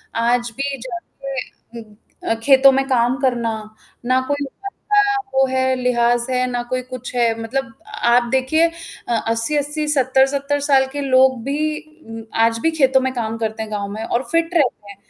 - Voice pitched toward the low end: No, very high, 255 Hz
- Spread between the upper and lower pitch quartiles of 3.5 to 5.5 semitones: No, average, 2.8 semitones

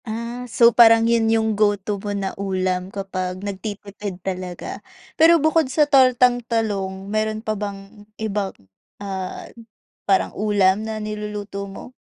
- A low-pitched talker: No, high, 210 Hz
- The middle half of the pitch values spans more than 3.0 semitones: No, narrow, 2.6 semitones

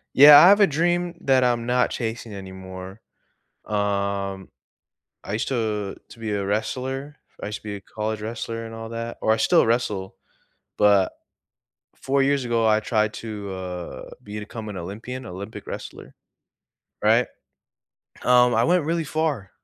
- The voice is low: Yes, low, 110 Hz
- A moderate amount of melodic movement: Yes, average, 3.8 semitones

